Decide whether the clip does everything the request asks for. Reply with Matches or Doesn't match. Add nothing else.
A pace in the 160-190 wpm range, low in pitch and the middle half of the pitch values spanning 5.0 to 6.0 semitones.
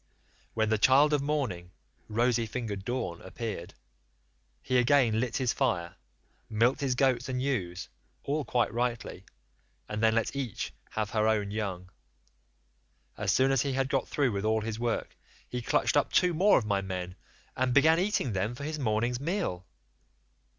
Doesn't match